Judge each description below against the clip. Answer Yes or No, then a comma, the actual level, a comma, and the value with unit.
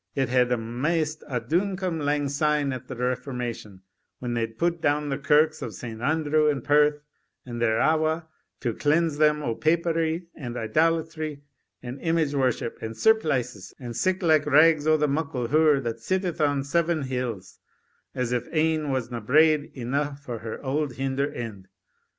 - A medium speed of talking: Yes, average, 160 wpm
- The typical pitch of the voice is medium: Yes, medium, 145 Hz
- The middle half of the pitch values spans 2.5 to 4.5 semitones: Yes, average, 4.2 semitones